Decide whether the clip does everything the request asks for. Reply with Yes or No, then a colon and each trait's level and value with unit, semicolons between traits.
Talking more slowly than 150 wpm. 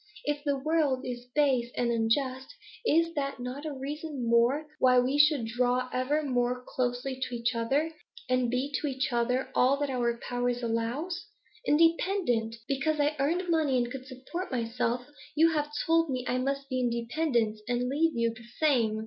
No: average, 175 wpm